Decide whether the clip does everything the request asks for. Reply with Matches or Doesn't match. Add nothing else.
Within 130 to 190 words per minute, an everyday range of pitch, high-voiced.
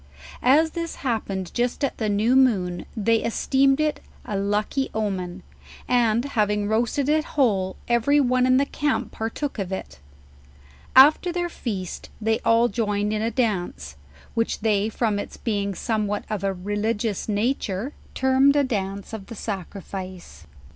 Matches